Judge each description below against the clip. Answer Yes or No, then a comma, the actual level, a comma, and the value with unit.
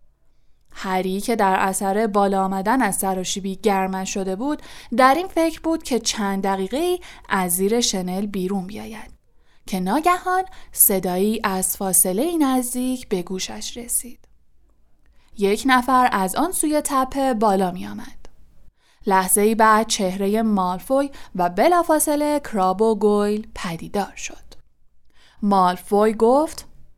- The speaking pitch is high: Yes, high, 210 Hz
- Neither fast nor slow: Yes, average, 125 wpm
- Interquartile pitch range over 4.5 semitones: Yes, average, 5.3 semitones